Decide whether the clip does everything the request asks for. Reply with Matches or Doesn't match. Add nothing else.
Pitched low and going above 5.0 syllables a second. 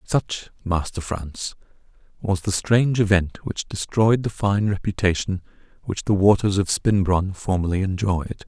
Doesn't match